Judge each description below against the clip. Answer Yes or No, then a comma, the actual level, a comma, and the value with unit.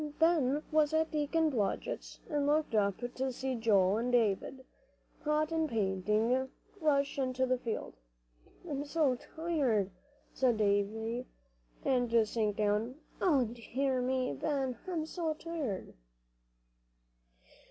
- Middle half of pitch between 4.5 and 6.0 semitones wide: Yes, average, 5.2 semitones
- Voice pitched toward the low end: No, very high, 260 Hz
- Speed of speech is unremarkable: No, slow, 120 wpm